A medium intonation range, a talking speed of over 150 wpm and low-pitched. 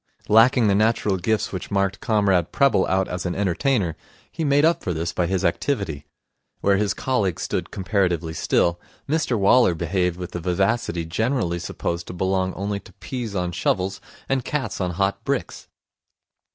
Yes: average, 4.0 semitones; average, 165 wpm; very low, 95 Hz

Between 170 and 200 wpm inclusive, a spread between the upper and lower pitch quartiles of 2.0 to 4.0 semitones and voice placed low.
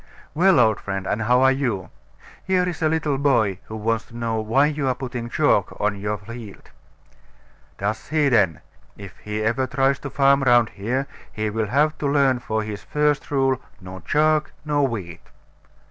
No: average, 180 wpm; average, 4.7 semitones; low, 120 Hz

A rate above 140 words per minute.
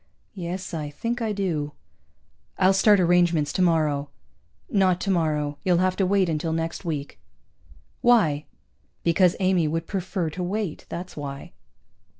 No: slow, 135 wpm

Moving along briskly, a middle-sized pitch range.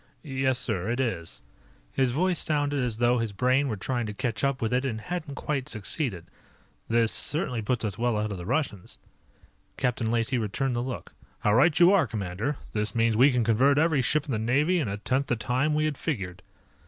Yes: fast, 210 wpm; average, 4.1 semitones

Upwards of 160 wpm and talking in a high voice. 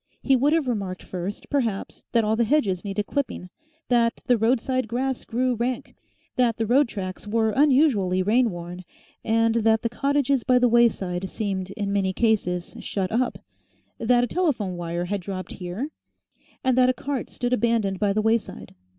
Yes: average, 170 wpm; high, 225 Hz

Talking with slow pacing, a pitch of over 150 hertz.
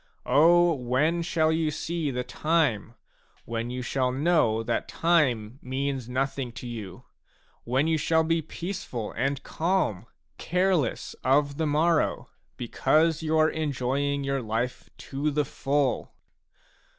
No: slow, 130 wpm; medium, 140 Hz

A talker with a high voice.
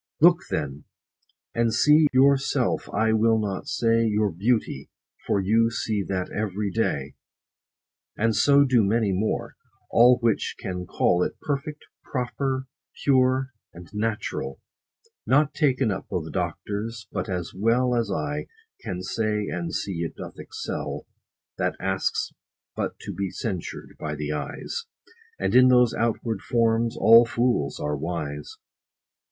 No: low, 110 Hz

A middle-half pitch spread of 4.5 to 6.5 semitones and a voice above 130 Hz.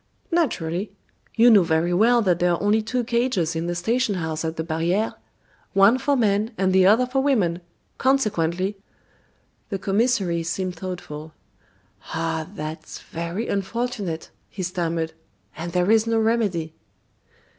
Yes: average, 5.1 semitones; high, 190 Hz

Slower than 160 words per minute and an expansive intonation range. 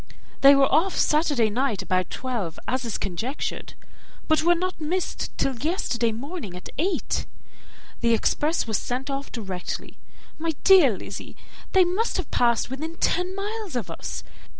Yes: average, 150 wpm; wide, 6.8 semitones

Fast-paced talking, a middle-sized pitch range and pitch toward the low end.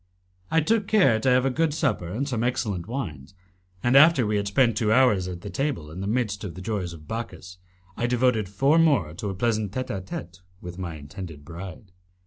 No: fast, 210 wpm; wide, 5.8 semitones; low, 105 Hz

